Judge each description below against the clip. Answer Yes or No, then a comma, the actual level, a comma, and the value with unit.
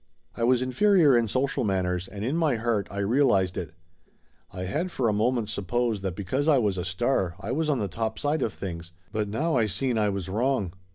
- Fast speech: Yes, fast, 220 wpm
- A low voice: Yes, low, 110 Hz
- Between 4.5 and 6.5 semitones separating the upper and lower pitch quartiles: Yes, average, 5.1 semitones